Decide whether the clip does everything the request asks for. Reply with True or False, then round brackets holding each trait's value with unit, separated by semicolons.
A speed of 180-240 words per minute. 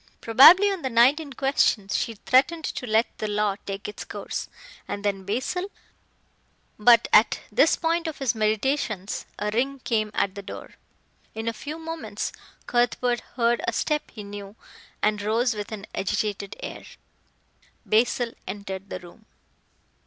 False (150 wpm)